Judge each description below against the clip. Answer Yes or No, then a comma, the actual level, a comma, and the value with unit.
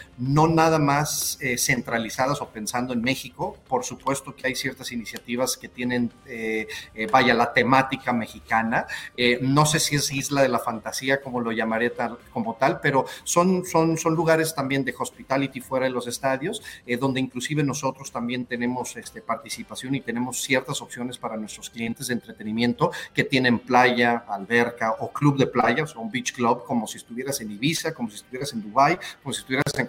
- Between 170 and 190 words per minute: Yes, average, 185 wpm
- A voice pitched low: Yes, low, 125 Hz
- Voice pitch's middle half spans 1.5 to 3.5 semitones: Yes, narrow, 2.5 semitones